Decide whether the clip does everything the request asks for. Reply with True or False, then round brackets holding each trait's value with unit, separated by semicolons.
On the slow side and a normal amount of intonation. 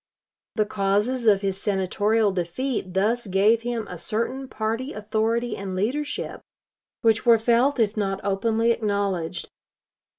True (130 wpm; 3.0 semitones)